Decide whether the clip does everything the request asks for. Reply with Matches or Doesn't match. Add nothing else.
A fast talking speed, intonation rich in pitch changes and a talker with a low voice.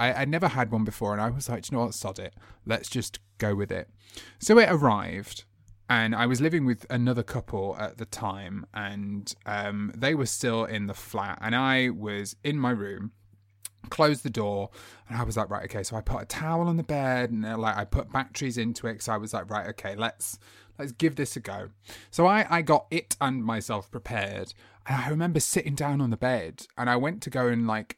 Doesn't match